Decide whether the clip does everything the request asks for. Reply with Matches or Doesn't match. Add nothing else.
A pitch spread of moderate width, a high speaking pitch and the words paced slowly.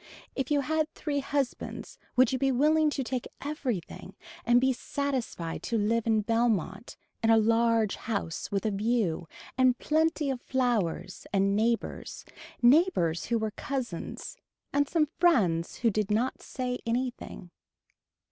Doesn't match